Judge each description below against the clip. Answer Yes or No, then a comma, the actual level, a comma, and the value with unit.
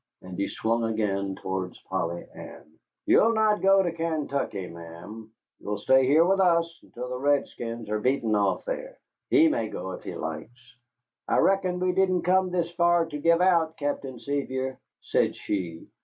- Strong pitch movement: Yes, wide, 8.8 semitones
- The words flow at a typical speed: Yes, average, 170 wpm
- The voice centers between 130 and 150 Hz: Yes, medium, 140 Hz